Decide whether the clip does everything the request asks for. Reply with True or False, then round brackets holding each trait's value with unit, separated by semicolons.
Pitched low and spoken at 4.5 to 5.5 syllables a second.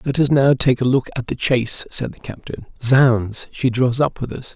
True (125 Hz; 4.8 syllables/s)